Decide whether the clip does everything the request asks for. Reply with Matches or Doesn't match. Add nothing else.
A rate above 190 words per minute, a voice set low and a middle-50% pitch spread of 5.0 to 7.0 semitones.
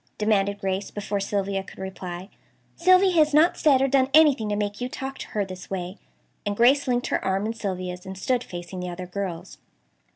Doesn't match